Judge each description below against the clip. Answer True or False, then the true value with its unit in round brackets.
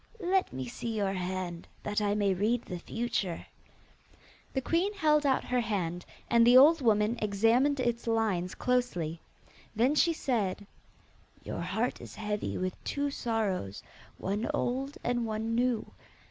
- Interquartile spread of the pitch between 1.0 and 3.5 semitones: False (4.4 semitones)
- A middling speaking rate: True (145 wpm)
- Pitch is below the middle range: False (225 Hz)